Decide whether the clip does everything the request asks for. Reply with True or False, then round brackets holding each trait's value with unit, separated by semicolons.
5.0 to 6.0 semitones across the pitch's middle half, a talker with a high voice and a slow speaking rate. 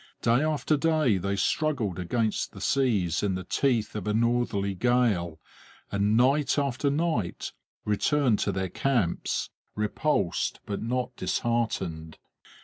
False (5.5 semitones; 115 Hz; 130 wpm)